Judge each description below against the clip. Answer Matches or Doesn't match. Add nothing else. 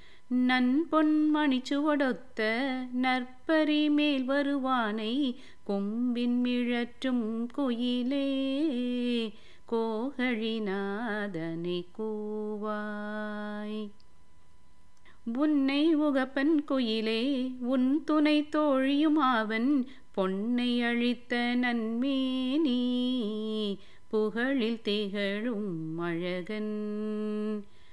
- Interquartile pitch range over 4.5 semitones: Doesn't match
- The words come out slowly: Matches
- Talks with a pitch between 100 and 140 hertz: Doesn't match